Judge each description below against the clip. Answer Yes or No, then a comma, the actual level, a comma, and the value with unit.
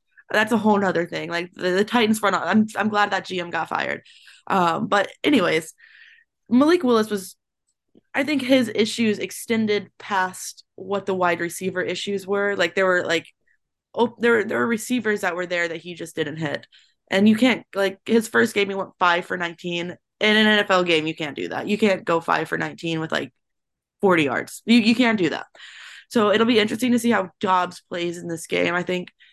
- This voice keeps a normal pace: No, fast, 210 wpm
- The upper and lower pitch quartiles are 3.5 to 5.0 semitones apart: Yes, average, 3.8 semitones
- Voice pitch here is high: Yes, high, 200 Hz